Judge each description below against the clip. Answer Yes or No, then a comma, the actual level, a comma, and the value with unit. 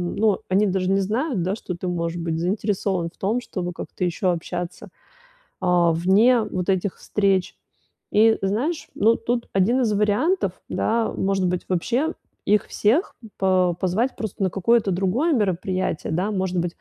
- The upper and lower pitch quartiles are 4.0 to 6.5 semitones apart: No, average, 3.5 semitones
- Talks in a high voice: Yes, high, 195 Hz